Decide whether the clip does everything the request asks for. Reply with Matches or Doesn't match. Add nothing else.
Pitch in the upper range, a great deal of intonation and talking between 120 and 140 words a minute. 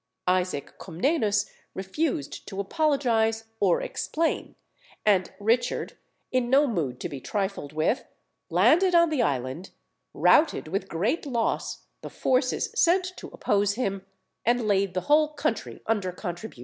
Matches